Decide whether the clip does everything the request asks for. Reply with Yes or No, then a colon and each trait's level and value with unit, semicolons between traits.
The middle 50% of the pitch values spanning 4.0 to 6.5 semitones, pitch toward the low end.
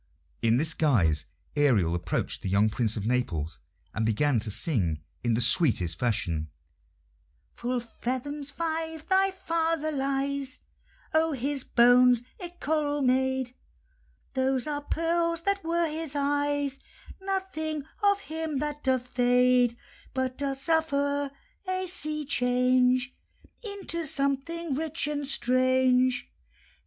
No: average, 4.8 semitones; very high, 270 Hz